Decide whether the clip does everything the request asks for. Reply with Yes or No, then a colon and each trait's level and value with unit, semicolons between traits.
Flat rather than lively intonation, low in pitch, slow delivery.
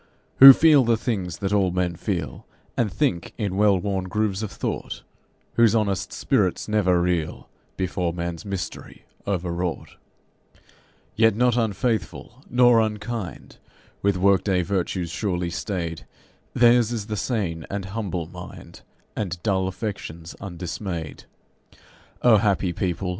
No: average, 3.5 semitones; very low, 95 Hz; slow, 130 wpm